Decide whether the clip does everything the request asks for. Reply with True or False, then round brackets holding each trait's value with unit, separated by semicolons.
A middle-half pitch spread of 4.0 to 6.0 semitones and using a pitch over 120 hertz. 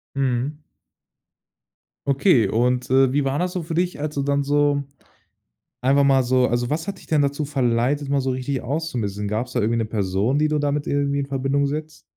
False (2.8 semitones; 140 Hz)